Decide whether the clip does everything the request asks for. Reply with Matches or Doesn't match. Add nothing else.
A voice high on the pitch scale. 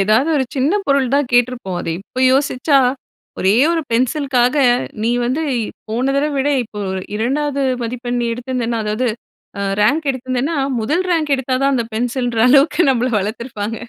Matches